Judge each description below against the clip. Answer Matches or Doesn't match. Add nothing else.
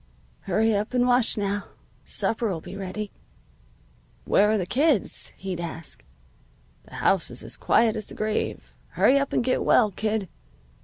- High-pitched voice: Matches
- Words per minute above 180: Doesn't match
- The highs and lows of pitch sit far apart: Doesn't match